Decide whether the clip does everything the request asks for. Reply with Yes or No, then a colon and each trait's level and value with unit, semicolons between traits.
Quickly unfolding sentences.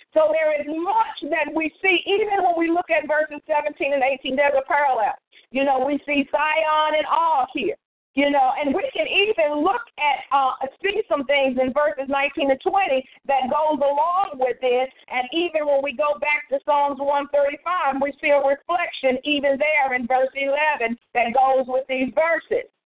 No: average, 195 wpm